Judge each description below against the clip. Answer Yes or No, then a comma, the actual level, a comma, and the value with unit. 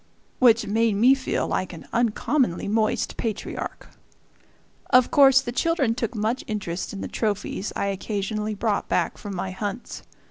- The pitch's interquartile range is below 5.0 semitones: Yes, average, 3.3 semitones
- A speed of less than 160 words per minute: Yes, average, 150 wpm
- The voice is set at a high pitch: Yes, high, 220 Hz